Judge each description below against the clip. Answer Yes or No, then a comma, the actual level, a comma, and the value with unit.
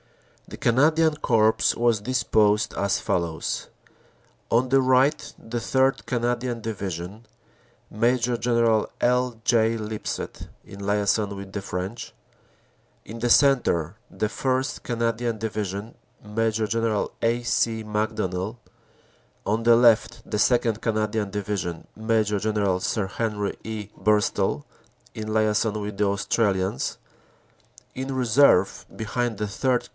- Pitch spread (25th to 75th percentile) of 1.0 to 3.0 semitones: Yes, narrow, 2.6 semitones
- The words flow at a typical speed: No, slow, 120 wpm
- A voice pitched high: No, low, 110 Hz